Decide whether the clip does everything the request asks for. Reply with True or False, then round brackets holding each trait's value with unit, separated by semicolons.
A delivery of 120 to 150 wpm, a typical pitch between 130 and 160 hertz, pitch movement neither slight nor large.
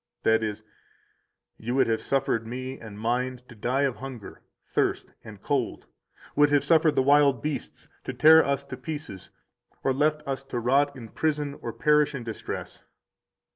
False (170 wpm; 135 Hz; 3.7 semitones)